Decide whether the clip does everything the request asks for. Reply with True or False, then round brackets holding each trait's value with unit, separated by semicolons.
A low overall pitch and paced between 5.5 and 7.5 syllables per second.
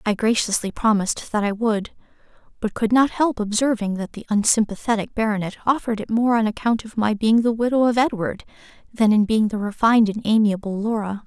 False (220 Hz; 5.8 syllables/s)